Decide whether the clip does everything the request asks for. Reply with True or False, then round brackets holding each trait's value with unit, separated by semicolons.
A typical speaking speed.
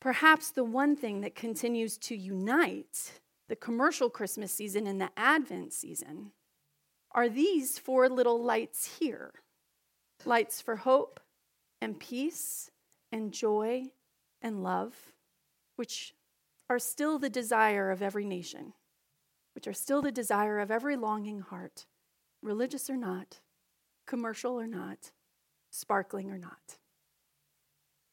False (120 wpm)